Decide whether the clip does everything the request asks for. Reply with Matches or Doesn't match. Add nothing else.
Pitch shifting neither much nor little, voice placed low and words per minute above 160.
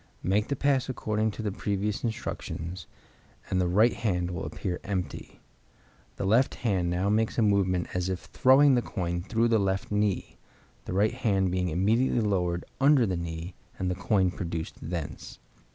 Matches